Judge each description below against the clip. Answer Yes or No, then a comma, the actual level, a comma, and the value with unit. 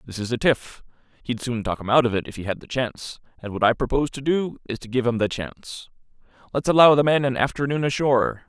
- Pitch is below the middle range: Yes, low, 125 Hz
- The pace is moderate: No, fast, 250 wpm